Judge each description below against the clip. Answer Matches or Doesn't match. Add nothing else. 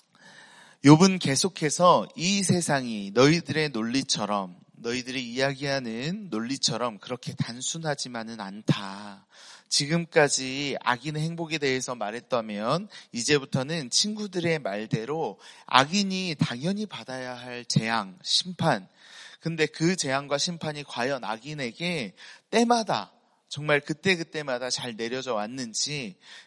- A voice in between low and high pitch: Matches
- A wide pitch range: Matches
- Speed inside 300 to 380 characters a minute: Doesn't match